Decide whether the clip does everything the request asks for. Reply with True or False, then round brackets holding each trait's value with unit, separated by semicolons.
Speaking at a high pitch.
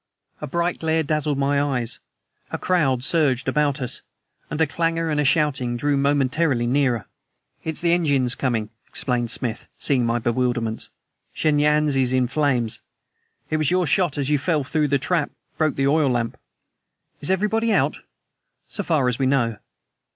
False (140 Hz)